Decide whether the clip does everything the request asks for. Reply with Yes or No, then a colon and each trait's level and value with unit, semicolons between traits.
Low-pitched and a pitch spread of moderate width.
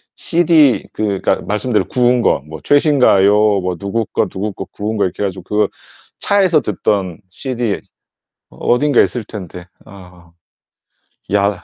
Yes: low, 105 Hz; average, 4.8 semitones